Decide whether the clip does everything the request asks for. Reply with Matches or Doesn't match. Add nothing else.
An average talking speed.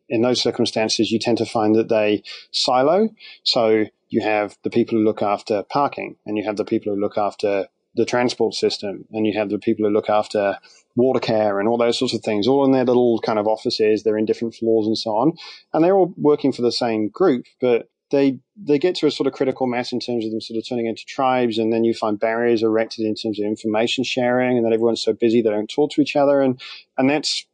Doesn't match